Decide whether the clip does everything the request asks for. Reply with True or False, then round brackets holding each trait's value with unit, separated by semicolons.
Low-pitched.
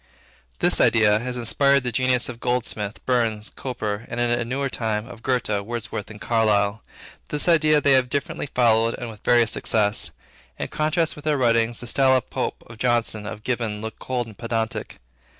True (120 Hz)